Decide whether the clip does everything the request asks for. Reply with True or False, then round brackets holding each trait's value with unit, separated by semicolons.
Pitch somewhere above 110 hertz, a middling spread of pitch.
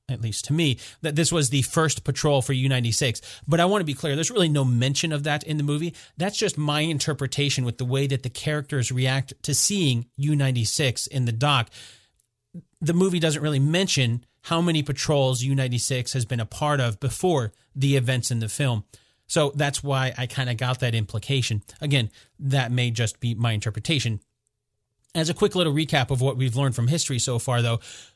True (135 Hz; 3.9 semitones)